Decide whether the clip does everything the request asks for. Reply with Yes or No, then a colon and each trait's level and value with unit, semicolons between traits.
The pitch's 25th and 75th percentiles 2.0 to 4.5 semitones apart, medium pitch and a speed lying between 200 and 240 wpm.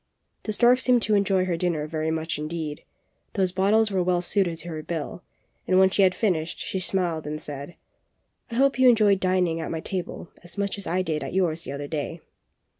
Yes: average, 3.6 semitones; medium, 180 Hz; fast, 205 wpm